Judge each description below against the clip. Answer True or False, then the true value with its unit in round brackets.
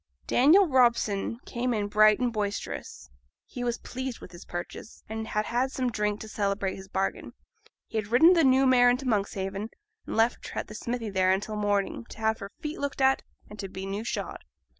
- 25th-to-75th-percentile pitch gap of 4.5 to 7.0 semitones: False (3.6 semitones)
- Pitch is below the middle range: False (220 Hz)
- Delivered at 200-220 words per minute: True (205 wpm)